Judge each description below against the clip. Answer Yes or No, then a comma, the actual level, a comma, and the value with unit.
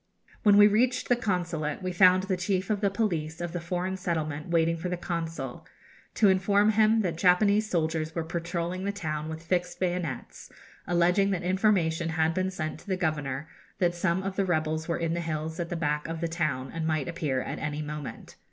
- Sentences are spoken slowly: No, fast, 205 wpm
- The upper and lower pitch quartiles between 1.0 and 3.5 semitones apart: Yes, average, 2.9 semitones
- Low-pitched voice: No, medium, 170 Hz